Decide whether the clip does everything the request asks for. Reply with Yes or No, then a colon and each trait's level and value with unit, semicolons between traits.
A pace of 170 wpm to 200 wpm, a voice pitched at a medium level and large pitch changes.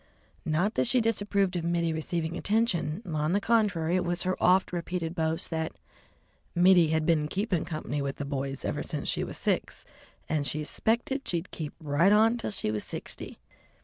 No: average, 180 wpm; medium, 170 Hz; average, 4.2 semitones